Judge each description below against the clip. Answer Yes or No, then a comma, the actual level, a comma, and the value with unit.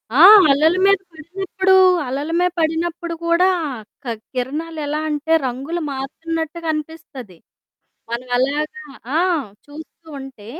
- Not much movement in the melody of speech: No, average, 3.6 semitones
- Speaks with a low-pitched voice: No, very high, 310 Hz